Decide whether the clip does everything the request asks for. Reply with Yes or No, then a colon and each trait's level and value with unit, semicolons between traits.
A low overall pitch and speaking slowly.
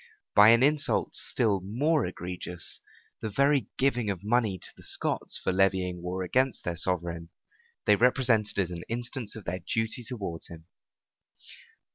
No: low, 105 Hz; average, 150 wpm